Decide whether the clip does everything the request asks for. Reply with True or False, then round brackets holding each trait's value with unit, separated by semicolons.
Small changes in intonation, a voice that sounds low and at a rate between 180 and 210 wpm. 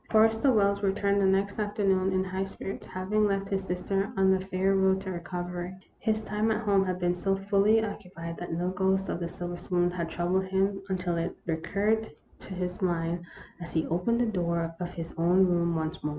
False (2.1 semitones; 190 Hz; 205 wpm)